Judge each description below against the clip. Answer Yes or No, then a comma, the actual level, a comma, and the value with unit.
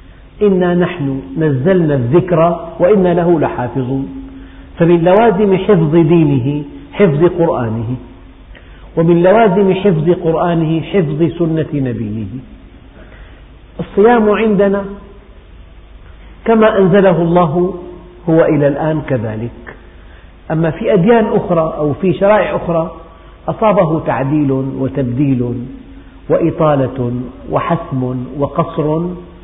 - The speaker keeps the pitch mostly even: No, wide, 5.4 semitones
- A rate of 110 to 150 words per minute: No, average, 90 wpm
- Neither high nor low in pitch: Yes, medium, 160 Hz